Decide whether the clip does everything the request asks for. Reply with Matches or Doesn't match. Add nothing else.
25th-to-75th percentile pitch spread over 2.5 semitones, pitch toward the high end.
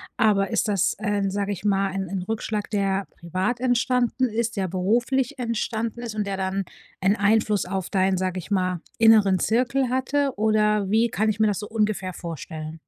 Matches